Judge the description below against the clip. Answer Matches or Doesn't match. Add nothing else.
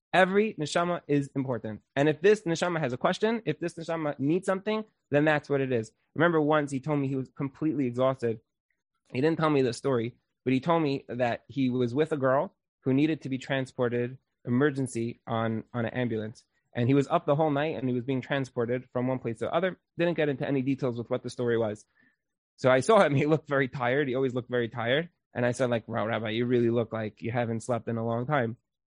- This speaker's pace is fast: Matches